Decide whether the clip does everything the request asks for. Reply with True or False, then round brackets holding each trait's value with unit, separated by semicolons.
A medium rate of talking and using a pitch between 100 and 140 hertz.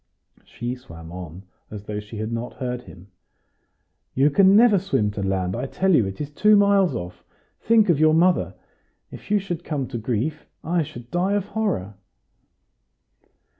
True (170 wpm; 135 Hz)